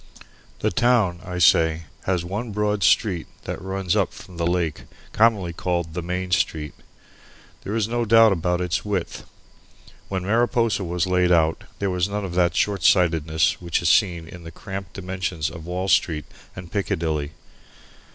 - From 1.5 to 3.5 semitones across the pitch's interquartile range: Yes, average, 2.8 semitones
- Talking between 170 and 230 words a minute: No, average, 160 wpm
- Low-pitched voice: Yes, very low, 90 Hz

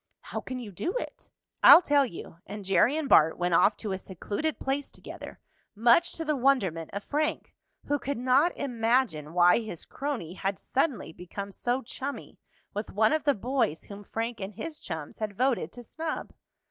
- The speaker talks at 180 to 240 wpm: Yes, average, 185 wpm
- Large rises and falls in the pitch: Yes, wide, 6.4 semitones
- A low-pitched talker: No, high, 235 Hz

